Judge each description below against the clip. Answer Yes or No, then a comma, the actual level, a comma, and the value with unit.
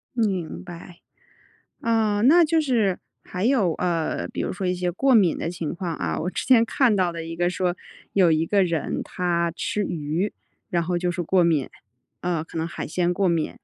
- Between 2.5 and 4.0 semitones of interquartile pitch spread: Yes, average, 3.4 semitones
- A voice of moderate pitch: Yes, medium, 180 Hz